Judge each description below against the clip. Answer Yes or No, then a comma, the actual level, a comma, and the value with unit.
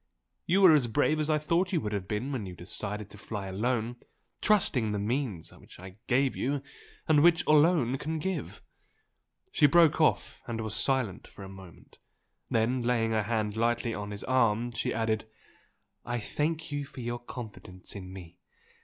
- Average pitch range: No, wide, 5.7 semitones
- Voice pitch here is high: No, low, 120 Hz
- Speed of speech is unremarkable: Yes, average, 180 wpm